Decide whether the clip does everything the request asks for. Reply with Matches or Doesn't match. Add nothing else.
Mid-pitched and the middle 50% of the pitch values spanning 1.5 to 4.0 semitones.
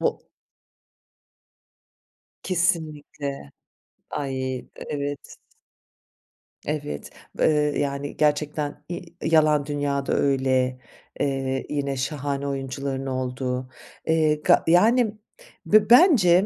Matches